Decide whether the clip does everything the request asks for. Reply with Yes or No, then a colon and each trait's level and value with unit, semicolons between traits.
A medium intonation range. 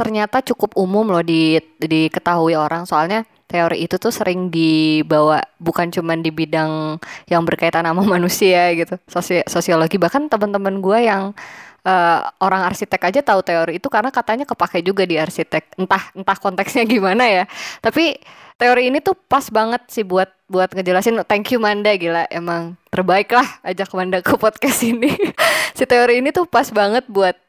Yes: average, 4.8 semitones